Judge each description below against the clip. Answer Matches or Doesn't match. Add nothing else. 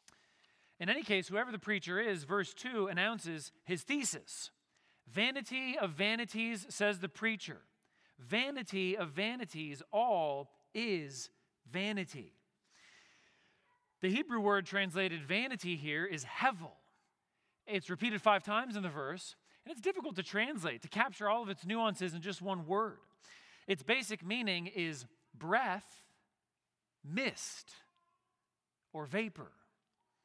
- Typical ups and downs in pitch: Matches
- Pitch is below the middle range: Doesn't match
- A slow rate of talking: Matches